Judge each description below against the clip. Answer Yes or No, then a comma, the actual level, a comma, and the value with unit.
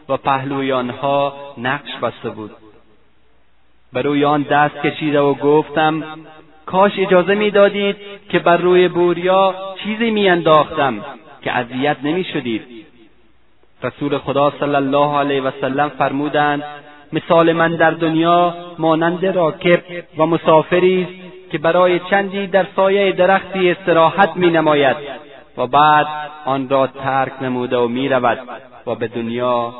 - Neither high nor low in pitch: Yes, medium, 155 Hz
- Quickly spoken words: No, average, 125 wpm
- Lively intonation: No, average, 4.2 semitones